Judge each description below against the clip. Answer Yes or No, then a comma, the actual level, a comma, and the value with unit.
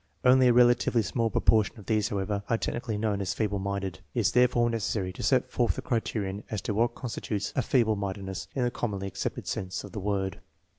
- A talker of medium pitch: No, low, 105 Hz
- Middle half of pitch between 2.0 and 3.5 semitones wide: Yes, average, 3.1 semitones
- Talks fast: Yes, fast, 210 wpm